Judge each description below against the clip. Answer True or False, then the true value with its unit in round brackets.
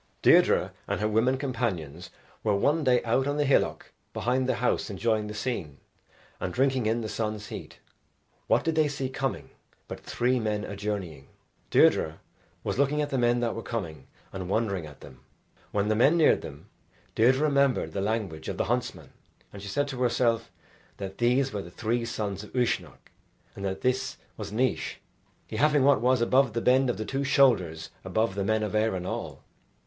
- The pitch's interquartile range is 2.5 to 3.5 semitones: False (4.5 semitones)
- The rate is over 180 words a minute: True (190 wpm)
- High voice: False (115 Hz)